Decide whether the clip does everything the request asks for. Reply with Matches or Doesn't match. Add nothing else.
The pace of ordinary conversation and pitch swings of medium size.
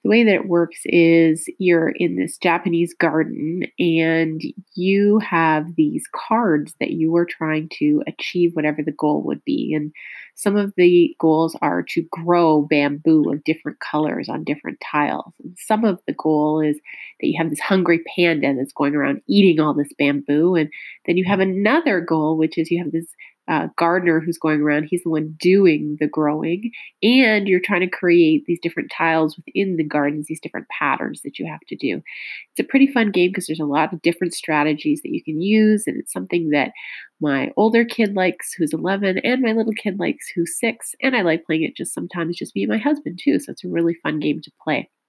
Doesn't match